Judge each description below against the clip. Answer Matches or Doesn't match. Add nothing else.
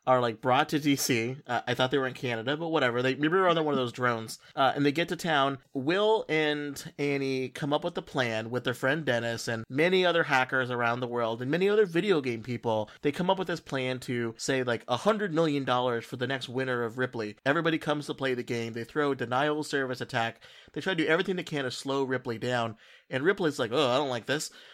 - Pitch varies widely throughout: Doesn't match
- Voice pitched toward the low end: Matches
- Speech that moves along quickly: Matches